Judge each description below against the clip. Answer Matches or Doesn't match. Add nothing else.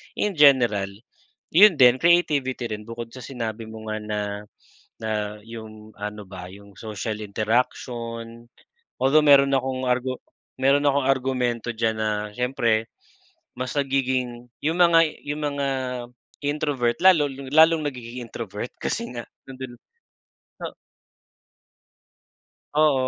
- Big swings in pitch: Doesn't match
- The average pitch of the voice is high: Doesn't match